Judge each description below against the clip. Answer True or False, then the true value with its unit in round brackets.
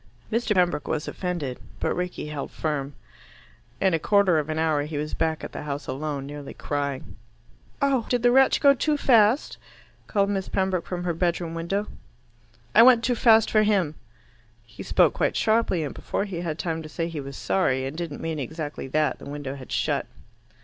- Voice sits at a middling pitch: True (165 Hz)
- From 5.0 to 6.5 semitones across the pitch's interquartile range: True (5.5 semitones)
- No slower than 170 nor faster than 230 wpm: True (190 wpm)